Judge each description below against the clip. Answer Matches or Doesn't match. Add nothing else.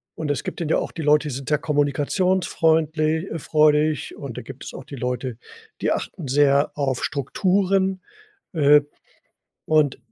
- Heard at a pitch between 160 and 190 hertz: Doesn't match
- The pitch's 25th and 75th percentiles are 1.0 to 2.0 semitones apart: Doesn't match